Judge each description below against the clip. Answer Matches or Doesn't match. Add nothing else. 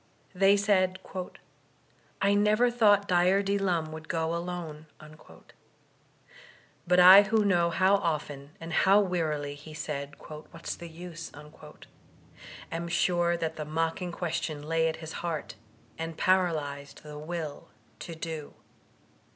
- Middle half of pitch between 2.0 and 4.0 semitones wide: Matches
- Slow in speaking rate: Matches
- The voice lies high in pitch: Doesn't match